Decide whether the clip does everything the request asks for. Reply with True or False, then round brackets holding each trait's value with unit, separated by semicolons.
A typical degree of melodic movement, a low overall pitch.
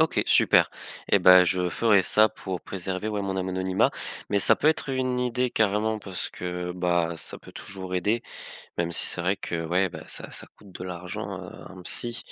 True (3.3 semitones; 95 Hz)